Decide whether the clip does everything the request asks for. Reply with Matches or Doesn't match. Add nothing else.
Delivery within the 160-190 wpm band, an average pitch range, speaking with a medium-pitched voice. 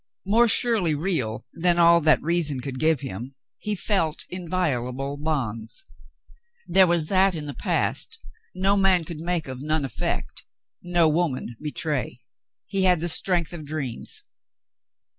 Doesn't match